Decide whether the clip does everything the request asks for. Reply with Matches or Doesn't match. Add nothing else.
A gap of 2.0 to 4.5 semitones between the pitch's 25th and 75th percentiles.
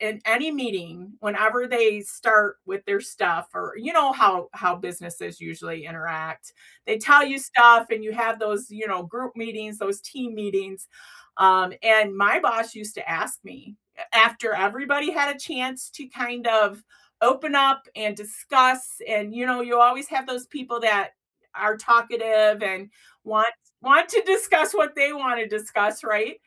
Matches